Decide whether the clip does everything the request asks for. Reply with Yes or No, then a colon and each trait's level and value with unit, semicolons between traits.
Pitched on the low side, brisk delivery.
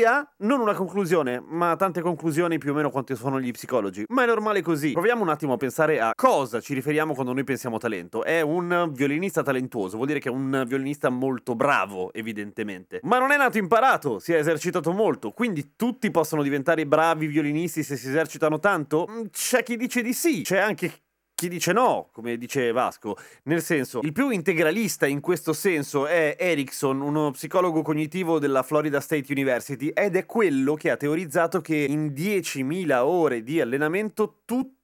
No: medium, 155 Hz; fast, 180 wpm